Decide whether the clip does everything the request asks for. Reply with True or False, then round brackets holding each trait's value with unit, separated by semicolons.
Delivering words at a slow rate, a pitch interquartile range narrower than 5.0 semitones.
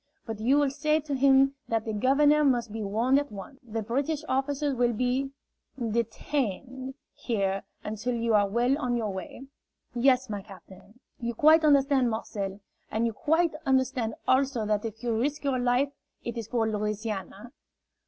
False (165 wpm; 3.8 semitones)